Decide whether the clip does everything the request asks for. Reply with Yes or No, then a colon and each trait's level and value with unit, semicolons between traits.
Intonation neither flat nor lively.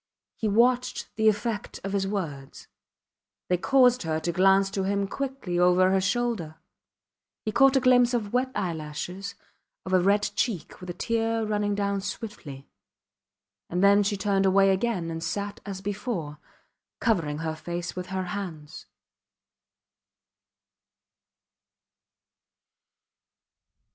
Yes: average, 3.5 semitones